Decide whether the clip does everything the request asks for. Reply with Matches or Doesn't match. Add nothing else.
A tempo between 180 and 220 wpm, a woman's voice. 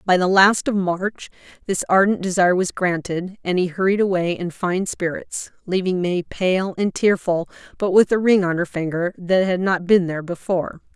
Matches